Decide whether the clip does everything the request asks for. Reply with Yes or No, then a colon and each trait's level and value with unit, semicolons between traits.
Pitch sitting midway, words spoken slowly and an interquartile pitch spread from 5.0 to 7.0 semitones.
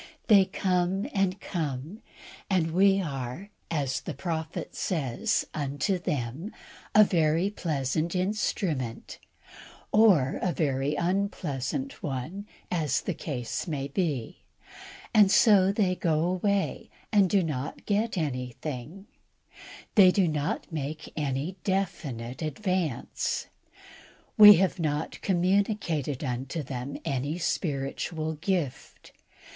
Yes: medium, 165 Hz; slow, 110 wpm; wide, 5.5 semitones